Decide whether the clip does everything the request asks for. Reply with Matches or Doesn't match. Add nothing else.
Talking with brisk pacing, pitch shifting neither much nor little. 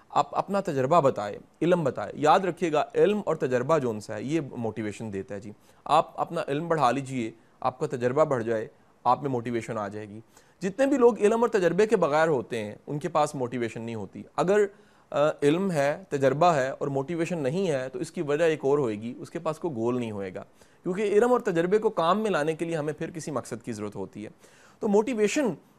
Doesn't match